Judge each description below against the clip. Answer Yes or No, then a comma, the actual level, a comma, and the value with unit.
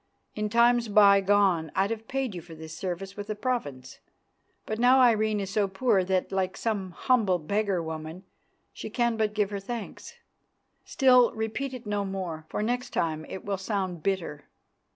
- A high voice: Yes, high, 200 Hz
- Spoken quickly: No, average, 170 wpm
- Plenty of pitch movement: No, average, 3.4 semitones